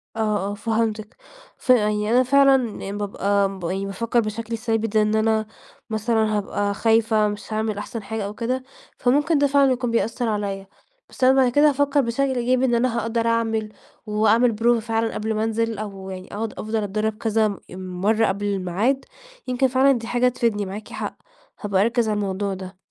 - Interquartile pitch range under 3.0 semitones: Yes, narrow, 2.6 semitones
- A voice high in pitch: Yes, high, 220 Hz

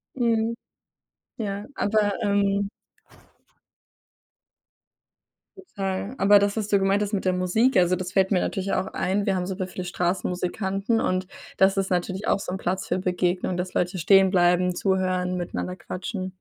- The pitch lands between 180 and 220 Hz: Yes, high, 190 Hz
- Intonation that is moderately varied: No, narrow, 1.8 semitones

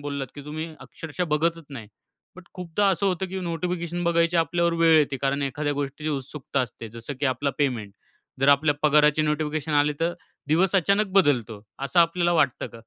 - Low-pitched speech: No, medium, 150 Hz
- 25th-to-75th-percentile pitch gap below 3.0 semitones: No, average, 3.4 semitones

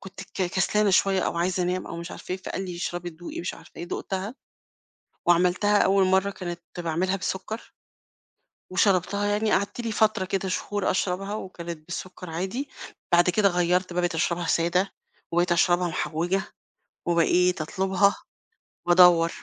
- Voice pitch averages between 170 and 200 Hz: Yes, medium, 185 Hz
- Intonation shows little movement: Yes, narrow, 2.0 semitones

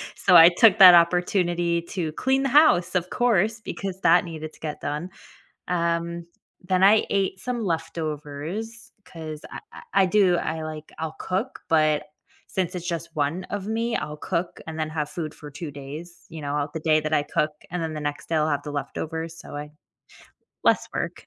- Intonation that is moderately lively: Yes, average, 3.3 semitones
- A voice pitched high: No, medium, 170 Hz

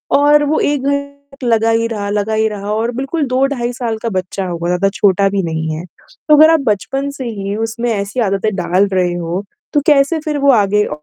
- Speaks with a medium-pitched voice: No, high, 220 Hz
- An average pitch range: No, wide, 5.9 semitones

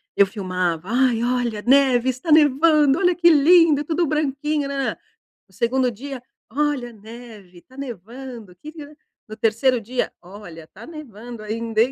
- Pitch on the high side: Yes, very high, 250 Hz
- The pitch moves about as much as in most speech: Yes, average, 5.0 semitones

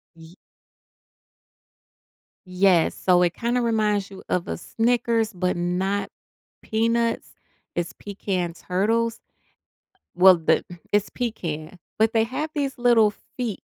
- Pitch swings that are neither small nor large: Yes, average, 4.2 semitones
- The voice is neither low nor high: No, high, 205 Hz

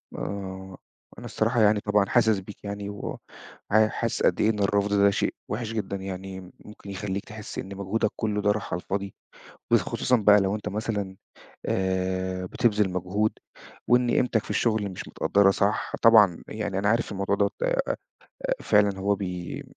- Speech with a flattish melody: Yes, narrow, 1.8 semitones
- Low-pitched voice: Yes, low, 100 Hz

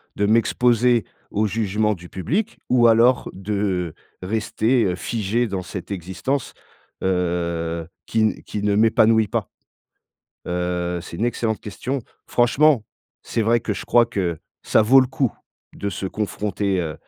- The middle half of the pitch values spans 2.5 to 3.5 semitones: No, average, 4.2 semitones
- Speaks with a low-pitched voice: Yes, low, 105 Hz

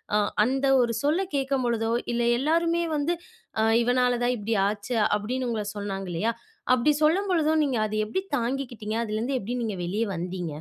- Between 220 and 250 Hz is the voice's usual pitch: Yes, high, 240 Hz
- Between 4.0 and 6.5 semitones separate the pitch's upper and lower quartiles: Yes, average, 4.6 semitones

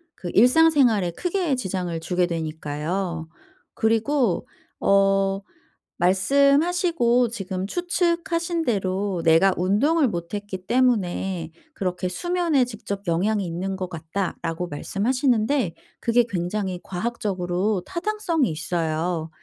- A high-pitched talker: Yes, high, 195 Hz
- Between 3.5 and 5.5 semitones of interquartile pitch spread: No, wide, 6.2 semitones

